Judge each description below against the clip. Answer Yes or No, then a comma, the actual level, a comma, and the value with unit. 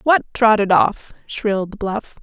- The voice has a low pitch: No, high, 210 Hz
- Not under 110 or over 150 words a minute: Yes, slow, 135 wpm